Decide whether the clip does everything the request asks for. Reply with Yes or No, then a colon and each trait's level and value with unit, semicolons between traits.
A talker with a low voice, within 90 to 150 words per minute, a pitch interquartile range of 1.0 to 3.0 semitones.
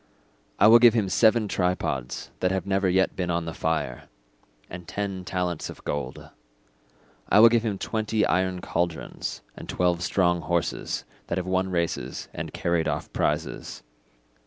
No: very low, 90 Hz; average, 160 wpm; narrow, 2.6 semitones